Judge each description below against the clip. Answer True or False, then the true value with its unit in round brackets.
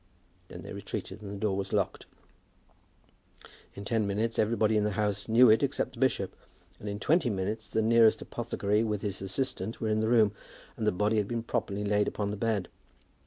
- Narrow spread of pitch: True (1.9 semitones)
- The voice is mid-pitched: False (105 Hz)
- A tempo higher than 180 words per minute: True (200 wpm)